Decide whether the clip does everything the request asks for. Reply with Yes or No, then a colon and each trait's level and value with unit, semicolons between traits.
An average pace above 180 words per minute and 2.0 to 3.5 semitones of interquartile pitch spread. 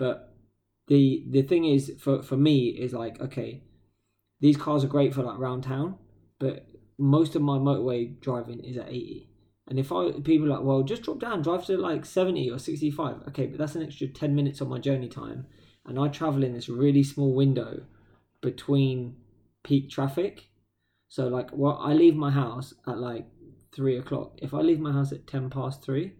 Yes: average, 200 wpm; average, 2.9 semitones